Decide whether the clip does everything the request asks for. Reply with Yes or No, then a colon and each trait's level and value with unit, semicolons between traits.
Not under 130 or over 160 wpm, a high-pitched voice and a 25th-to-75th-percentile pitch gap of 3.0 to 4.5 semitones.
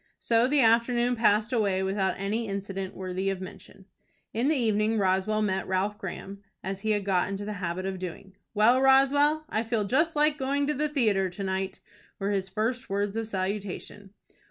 No: average, 185 wpm; high, 205 Hz; average, 3.7 semitones